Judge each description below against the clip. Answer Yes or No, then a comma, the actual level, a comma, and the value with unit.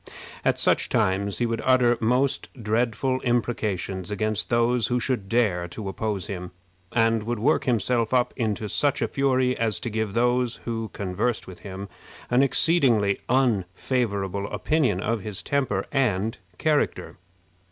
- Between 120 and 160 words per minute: Yes, average, 145 wpm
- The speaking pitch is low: Yes, low, 115 Hz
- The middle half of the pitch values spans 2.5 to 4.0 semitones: Yes, average, 3.7 semitones